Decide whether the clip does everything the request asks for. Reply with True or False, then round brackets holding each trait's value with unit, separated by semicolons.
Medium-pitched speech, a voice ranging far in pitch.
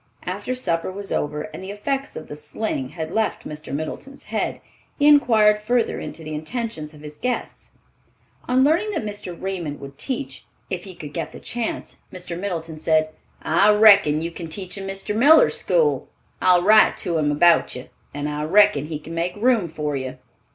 True (180 Hz; 5.8 semitones)